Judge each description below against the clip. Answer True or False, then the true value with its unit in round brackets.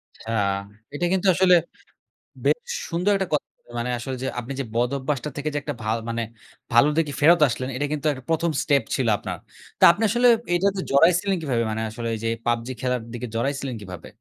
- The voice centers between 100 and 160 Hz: True (140 Hz)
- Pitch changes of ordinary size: False (6.0 semitones)